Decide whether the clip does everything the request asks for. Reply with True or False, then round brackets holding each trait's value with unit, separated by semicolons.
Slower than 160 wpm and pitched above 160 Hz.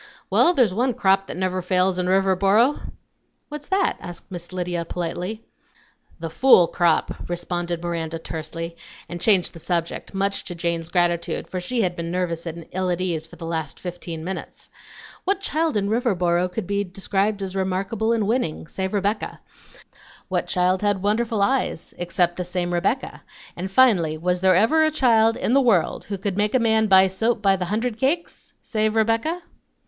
False (175 wpm; 190 Hz)